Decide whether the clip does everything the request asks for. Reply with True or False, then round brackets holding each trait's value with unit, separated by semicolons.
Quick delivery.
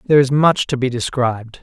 True (220 wpm)